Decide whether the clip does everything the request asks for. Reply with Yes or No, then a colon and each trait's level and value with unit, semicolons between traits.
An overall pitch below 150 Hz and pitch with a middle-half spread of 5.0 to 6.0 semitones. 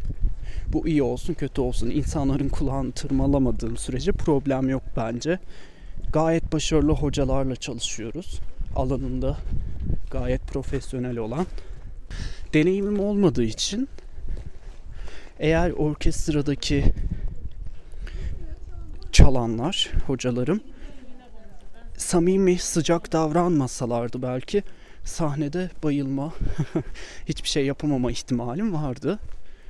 Yes: low, 135 Hz; average, 5.3 semitones